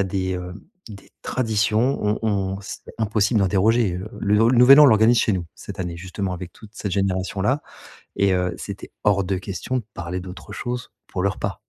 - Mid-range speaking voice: No, low, 100 Hz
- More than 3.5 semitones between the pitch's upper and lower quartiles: No, average, 3.0 semitones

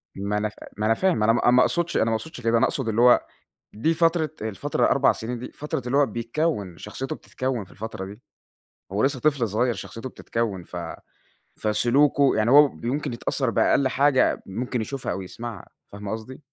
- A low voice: Yes, low, 120 Hz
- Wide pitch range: No, average, 4.3 semitones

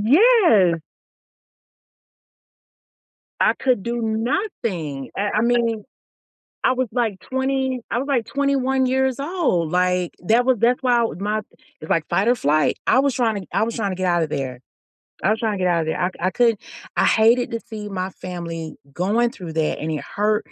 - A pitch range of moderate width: No, wide, 5.8 semitones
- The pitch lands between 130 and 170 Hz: No, high, 220 Hz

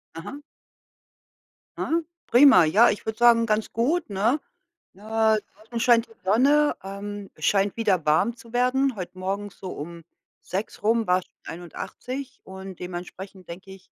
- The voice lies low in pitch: No, high, 205 Hz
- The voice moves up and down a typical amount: Yes, average, 4.0 semitones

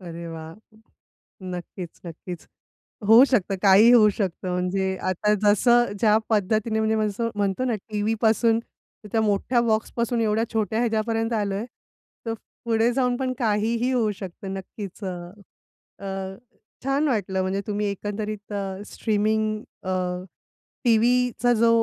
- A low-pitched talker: No, high, 215 Hz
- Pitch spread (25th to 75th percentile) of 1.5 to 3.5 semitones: Yes, average, 2.9 semitones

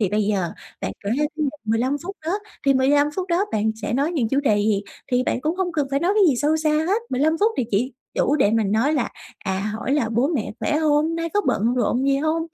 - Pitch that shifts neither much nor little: No, wide, 6.1 semitones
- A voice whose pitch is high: Yes, very high, 275 Hz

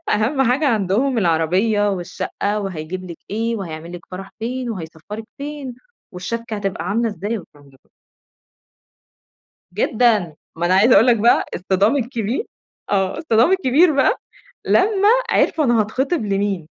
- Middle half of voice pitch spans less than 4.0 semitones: No, average, 5.0 semitones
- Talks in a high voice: Yes, high, 215 Hz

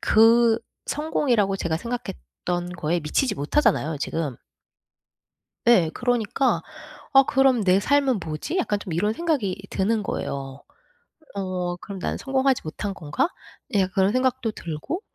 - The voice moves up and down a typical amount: No, wide, 6.4 semitones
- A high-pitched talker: Yes, high, 200 Hz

